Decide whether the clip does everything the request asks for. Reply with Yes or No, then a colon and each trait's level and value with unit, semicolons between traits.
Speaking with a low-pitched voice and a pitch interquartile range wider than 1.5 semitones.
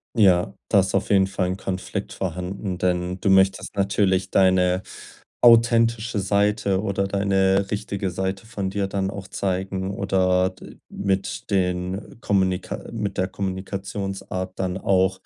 No: very low, 95 Hz; narrow, 1.2 semitones